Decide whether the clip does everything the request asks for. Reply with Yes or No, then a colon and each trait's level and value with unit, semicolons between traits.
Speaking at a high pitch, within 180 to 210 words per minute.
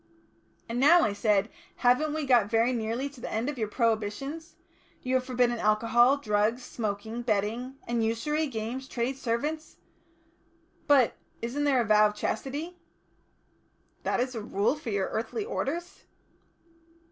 No: high, 240 Hz; average, 145 wpm